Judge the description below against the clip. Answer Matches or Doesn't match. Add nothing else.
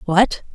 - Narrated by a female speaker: Matches